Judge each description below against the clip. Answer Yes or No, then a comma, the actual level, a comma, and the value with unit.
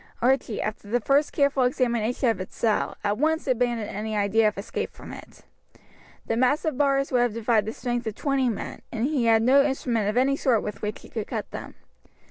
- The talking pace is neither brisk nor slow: No, fast, 210 wpm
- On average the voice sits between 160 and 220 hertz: No, high, 240 Hz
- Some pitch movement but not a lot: Yes, average, 3.7 semitones